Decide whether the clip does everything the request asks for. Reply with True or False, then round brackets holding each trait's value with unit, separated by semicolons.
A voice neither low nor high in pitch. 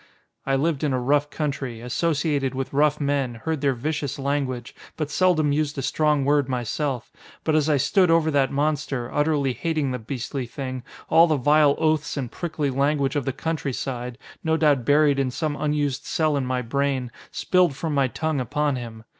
True (145 Hz)